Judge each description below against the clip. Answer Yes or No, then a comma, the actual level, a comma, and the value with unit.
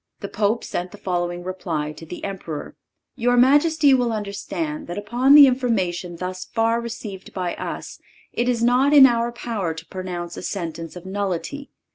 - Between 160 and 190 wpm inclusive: Yes, average, 170 wpm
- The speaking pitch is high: Yes, high, 205 Hz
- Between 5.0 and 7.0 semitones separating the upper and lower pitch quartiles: Yes, wide, 5.5 semitones